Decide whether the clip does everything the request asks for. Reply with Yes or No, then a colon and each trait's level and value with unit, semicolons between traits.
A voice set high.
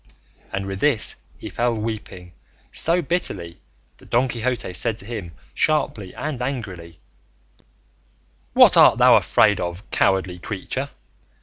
No: low, 110 Hz